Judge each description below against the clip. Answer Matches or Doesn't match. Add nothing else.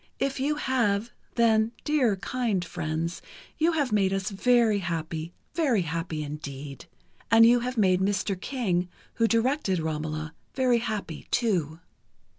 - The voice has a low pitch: Doesn't match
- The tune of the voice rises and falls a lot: Matches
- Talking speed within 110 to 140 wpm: Matches